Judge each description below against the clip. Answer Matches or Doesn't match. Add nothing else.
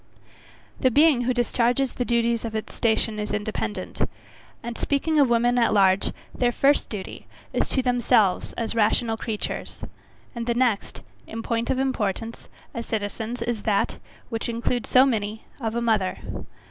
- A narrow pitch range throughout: Matches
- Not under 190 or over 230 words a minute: Doesn't match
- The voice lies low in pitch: Doesn't match